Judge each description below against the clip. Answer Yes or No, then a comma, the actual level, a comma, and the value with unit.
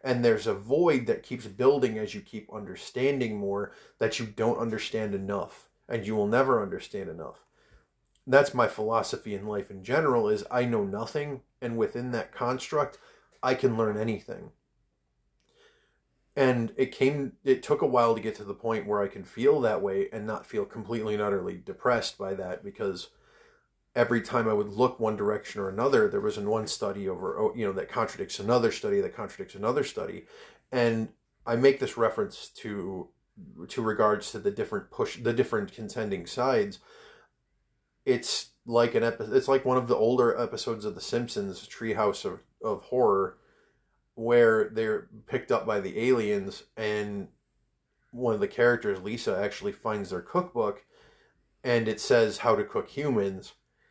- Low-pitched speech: Yes, low, 120 Hz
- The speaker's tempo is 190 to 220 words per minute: No, average, 170 wpm